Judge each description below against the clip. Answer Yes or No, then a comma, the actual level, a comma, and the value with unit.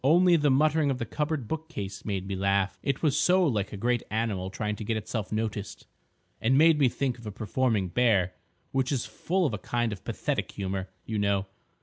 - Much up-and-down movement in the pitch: Yes, wide, 5.7 semitones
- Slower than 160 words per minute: No, fast, 205 wpm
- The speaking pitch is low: Yes, low, 115 Hz